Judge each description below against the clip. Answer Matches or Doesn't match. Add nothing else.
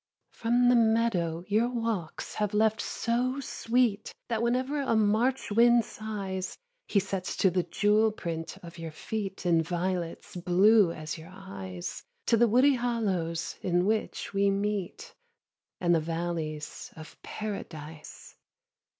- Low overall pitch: Doesn't match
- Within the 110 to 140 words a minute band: Matches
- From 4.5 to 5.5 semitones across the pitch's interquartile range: Matches